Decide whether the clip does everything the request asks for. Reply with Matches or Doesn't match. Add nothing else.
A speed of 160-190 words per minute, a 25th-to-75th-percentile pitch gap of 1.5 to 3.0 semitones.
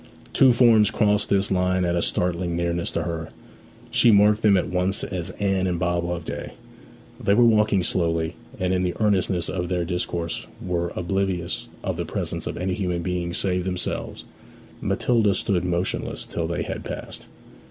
Matches